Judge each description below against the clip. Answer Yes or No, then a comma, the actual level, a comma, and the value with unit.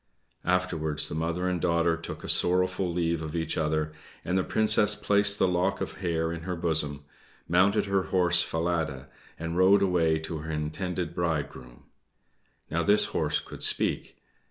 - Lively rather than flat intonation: No, narrow, 2.5 semitones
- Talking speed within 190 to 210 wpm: No, average, 160 wpm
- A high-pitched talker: No, very low, 85 Hz